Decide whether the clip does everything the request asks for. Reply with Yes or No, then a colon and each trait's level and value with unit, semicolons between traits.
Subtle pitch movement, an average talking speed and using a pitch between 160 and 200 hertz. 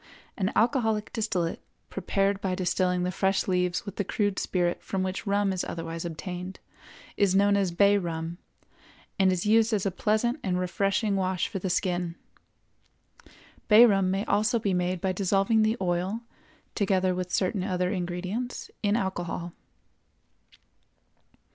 Yes: narrow, 2.2 semitones; average, 150 wpm; high, 190 Hz